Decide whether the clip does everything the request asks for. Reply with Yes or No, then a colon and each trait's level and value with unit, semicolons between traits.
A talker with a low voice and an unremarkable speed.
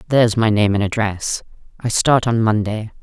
Yes: low, 110 Hz; average, 180 wpm